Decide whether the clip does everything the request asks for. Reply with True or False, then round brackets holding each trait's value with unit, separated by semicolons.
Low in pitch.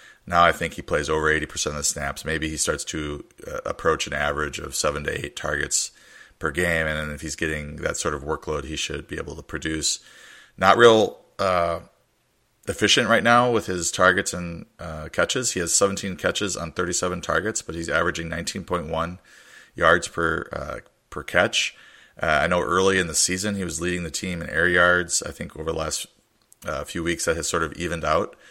True (85 Hz)